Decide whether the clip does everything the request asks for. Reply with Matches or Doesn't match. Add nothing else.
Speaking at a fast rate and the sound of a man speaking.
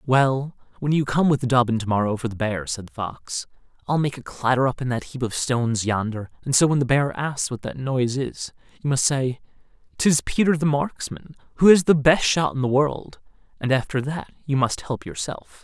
Matches